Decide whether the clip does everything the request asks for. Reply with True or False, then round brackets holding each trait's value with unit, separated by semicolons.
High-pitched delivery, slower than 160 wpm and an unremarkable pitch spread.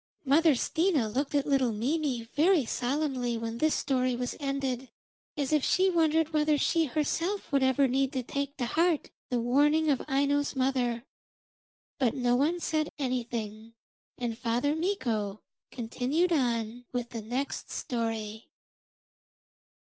True (265 Hz; 140 wpm; 3.9 semitones)